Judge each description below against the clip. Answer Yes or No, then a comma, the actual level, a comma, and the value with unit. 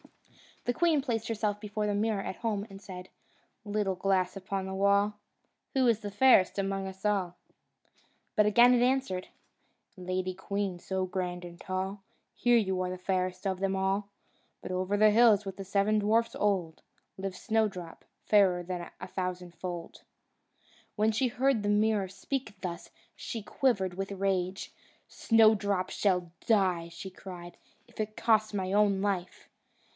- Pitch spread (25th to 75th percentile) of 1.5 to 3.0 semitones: Yes, narrow, 2.5 semitones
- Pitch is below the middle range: No, high, 195 Hz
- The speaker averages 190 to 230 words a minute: No, average, 150 wpm